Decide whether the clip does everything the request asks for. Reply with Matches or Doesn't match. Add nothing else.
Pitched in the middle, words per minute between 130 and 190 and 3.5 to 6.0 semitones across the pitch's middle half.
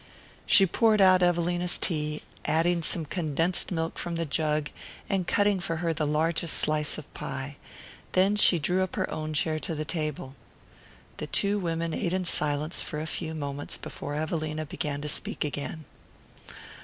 Doesn't match